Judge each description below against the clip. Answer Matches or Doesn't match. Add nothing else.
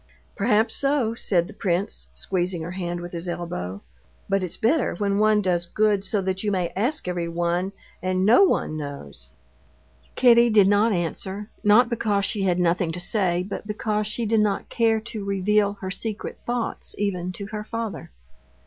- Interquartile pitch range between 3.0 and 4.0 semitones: Matches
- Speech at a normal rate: Matches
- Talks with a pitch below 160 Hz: Doesn't match